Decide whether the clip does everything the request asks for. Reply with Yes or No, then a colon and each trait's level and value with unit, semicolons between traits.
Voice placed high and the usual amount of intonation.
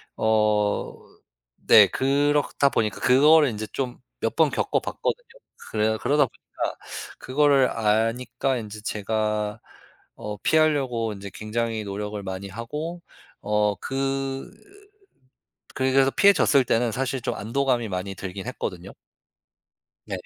No: low, 115 Hz; average, 4.4 semitones